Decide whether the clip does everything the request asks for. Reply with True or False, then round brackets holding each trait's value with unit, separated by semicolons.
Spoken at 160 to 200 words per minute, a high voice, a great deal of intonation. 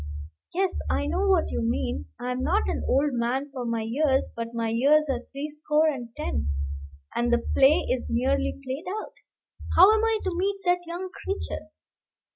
True (180 wpm; 275 Hz; 6.4 semitones)